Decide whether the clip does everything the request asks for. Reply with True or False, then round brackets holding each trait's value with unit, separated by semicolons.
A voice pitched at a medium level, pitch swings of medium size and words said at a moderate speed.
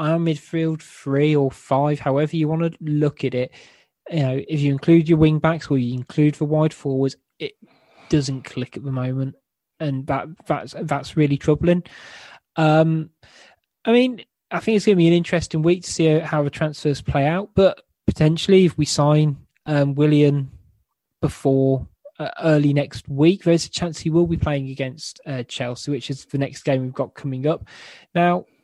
True (150 Hz; 3.1 semitones; 185 wpm)